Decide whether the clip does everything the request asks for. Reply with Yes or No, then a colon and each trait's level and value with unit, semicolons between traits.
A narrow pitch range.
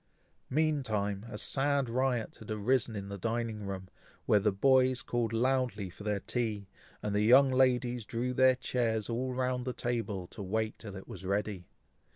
No: average, 3.7 semitones